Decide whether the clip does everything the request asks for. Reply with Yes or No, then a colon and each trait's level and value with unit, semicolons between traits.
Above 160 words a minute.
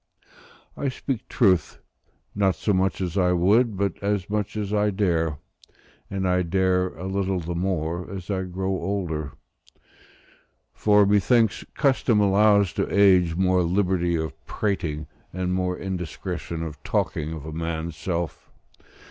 No: average, 140 wpm